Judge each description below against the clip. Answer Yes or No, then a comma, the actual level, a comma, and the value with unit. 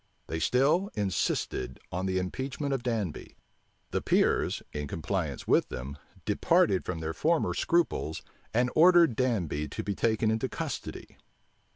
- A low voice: Yes, low, 105 Hz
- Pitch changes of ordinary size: No, wide, 8.4 semitones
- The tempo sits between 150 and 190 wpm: No, average, 140 wpm